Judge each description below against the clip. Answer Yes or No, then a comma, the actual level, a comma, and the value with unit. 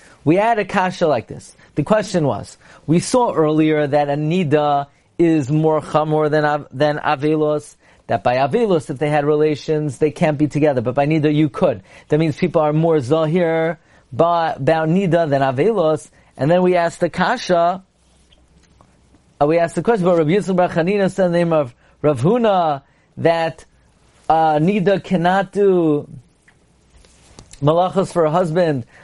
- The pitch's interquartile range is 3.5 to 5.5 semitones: No, average, 2.8 semitones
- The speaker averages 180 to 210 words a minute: No, average, 165 wpm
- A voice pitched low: No, medium, 160 Hz